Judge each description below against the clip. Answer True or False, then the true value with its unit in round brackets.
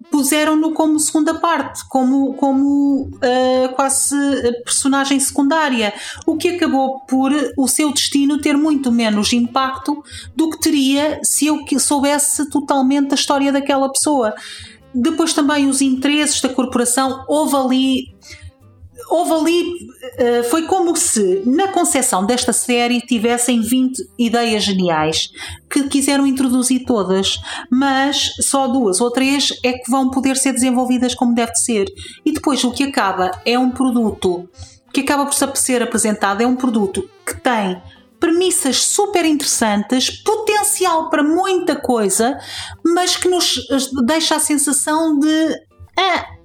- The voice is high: True (270 Hz)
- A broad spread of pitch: False (3.5 semitones)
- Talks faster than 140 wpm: False (135 wpm)